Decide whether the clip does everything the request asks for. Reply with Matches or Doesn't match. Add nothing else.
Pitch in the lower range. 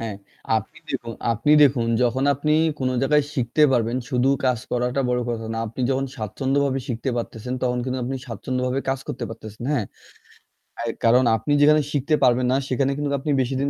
Matches